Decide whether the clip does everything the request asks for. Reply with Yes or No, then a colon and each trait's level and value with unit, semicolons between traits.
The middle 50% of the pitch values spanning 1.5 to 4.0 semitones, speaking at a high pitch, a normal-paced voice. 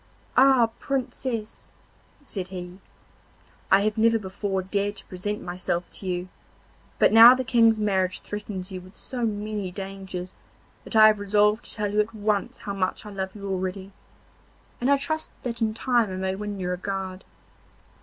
Yes: narrow, 2.6 semitones; high, 205 Hz; average, 170 wpm